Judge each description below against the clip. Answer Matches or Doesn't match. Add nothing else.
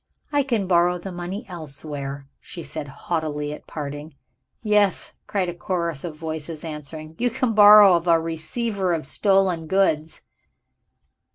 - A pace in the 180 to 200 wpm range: Doesn't match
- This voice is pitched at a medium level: Matches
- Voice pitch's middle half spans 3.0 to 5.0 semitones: Matches